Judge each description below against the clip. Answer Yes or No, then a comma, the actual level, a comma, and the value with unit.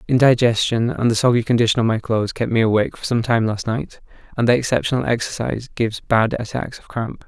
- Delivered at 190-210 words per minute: Yes, fast, 205 wpm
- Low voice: Yes, low, 115 Hz